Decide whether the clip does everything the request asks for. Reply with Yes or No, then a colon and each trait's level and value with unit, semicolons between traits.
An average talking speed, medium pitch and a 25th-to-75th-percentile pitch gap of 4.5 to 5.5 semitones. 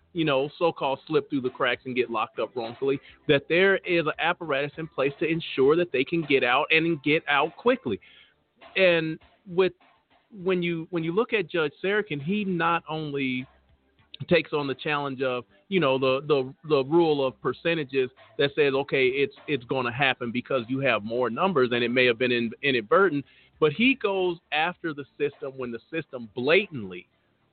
Yes: average, 185 wpm; medium, 145 Hz; average, 4.9 semitones